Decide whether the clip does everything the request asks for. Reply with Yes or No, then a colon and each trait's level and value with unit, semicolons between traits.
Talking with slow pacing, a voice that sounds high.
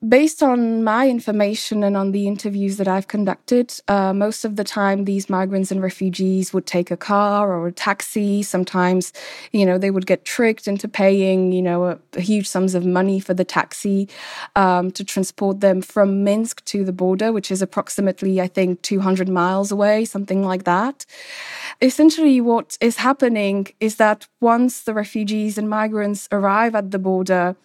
No: average, 180 wpm; high, 200 Hz